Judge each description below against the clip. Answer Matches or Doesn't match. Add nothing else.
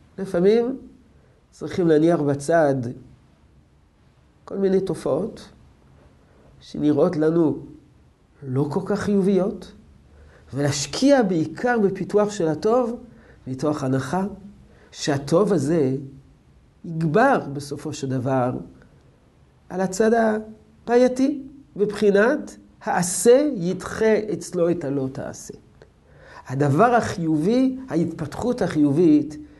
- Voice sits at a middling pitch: Matches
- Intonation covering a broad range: Matches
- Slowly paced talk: Matches